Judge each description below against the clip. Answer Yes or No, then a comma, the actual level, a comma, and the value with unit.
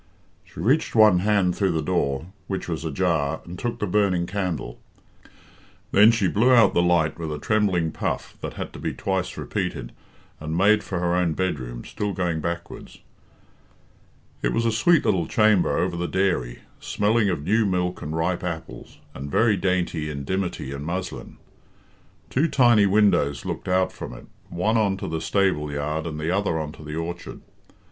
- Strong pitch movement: No, average, 4.2 semitones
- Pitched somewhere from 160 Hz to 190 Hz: No, very low, 90 Hz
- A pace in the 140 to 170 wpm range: No, average, 180 wpm